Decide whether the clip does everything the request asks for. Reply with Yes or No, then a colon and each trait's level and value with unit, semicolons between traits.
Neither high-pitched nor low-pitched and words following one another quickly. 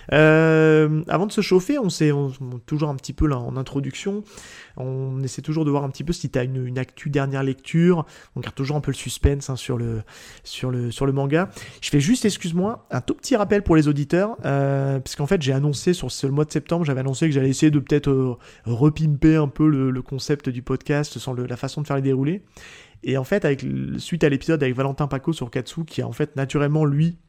Yes: medium, 145 Hz; fast, 235 wpm